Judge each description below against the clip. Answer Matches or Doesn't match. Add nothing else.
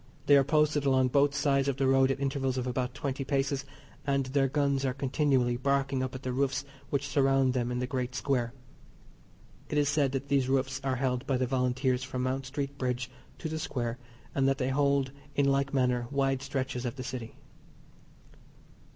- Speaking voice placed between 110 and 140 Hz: Matches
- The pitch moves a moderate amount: Doesn't match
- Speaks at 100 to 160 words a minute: Doesn't match